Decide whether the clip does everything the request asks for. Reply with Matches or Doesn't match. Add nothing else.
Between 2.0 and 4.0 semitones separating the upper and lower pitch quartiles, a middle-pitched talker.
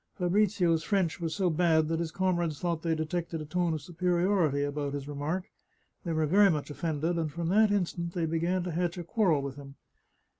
Matches